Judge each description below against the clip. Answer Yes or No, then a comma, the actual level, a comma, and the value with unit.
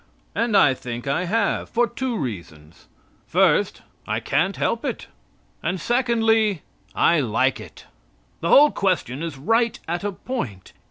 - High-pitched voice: No, medium, 180 Hz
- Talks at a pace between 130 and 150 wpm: Yes, average, 145 wpm